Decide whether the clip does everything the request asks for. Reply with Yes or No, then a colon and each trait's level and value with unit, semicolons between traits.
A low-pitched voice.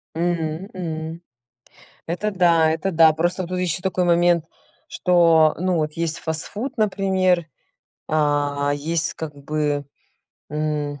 No: medium, 165 Hz